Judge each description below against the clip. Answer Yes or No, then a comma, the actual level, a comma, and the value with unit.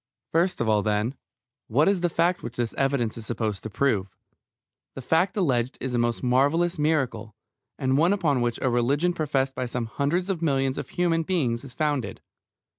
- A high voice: No, low, 135 Hz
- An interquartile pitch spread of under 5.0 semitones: No, wide, 5.6 semitones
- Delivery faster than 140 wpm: Yes, average, 190 wpm